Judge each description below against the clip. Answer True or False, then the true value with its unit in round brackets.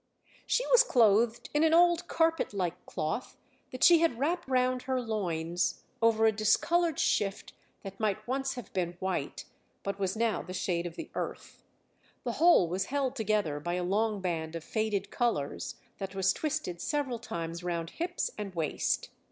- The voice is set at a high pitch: True (215 Hz)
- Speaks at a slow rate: False (170 wpm)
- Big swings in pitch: True (6.6 semitones)